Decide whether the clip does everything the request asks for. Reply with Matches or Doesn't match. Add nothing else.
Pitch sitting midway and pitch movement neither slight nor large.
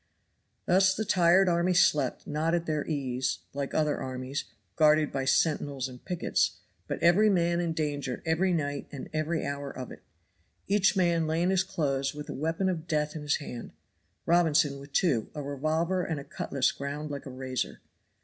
Matches